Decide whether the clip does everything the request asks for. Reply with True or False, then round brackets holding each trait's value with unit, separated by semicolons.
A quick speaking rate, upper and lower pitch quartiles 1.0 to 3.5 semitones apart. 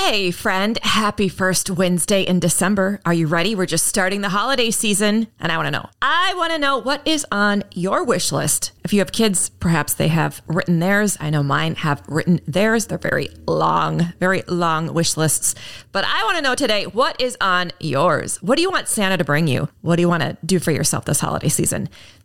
False (210 wpm; 4.2 semitones)